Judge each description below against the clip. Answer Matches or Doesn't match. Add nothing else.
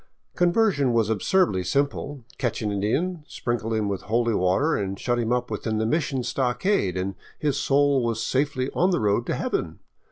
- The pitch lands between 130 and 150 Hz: Doesn't match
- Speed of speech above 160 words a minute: Matches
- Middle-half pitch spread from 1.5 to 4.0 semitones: Doesn't match